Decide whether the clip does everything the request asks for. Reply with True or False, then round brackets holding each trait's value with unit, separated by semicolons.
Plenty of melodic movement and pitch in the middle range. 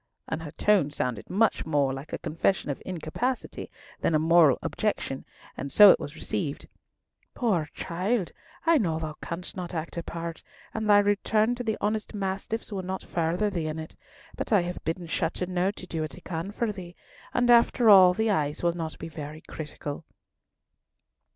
False (4.5 semitones; 175 Hz)